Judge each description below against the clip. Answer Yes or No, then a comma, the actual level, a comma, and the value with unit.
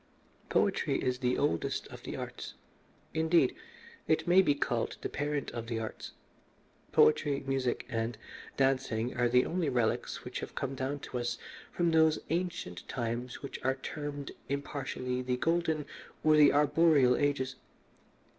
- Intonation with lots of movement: No, average, 3.4 semitones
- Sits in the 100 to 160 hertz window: Yes, low, 135 Hz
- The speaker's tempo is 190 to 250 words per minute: No, average, 145 wpm